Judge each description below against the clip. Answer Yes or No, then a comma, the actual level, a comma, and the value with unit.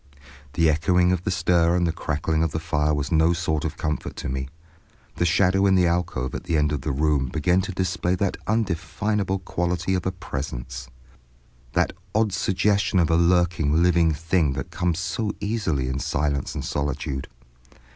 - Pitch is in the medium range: No, very low, 85 Hz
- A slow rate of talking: No, average, 175 wpm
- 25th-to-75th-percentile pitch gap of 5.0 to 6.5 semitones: No, average, 3.6 semitones